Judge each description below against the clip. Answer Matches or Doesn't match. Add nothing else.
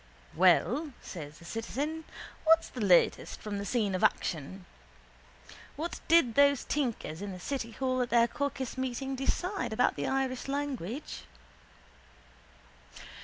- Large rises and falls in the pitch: Matches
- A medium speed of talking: Doesn't match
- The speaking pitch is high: Matches